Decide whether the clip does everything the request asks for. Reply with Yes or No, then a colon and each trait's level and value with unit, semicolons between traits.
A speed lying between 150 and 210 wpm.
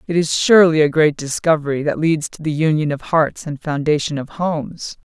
Yes: average, 200 wpm